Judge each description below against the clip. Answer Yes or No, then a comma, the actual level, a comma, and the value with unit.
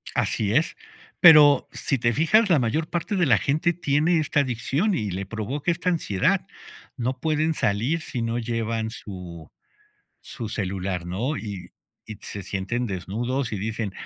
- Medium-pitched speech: No, low, 120 Hz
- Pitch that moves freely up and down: Yes, wide, 7.0 semitones